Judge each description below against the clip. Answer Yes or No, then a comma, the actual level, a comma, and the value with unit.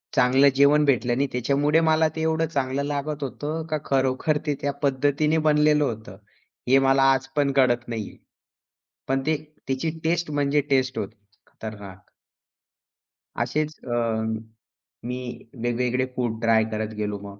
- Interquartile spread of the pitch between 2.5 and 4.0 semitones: Yes, average, 3.6 semitones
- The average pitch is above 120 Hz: Yes, low, 135 Hz